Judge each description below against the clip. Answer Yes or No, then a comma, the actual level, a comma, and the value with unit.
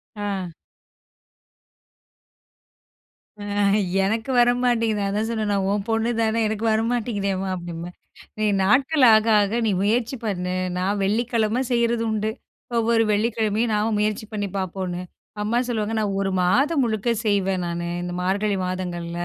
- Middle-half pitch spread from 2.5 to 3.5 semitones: Yes, average, 2.8 semitones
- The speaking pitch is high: Yes, high, 210 Hz